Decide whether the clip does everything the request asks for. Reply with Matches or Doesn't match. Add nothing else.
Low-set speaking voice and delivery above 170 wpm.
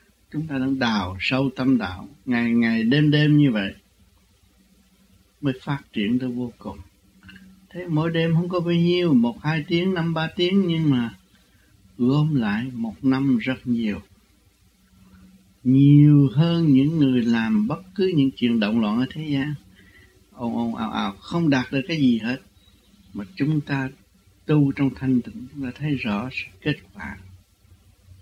Doesn't match